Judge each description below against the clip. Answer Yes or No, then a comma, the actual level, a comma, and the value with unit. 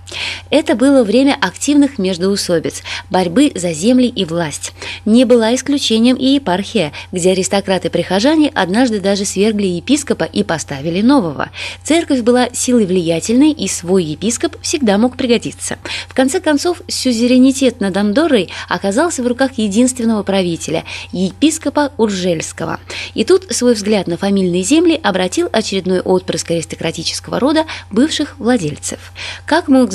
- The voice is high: Yes, high, 220 Hz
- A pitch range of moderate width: No, wide, 6.3 semitones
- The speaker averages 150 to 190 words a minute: No, average, 125 wpm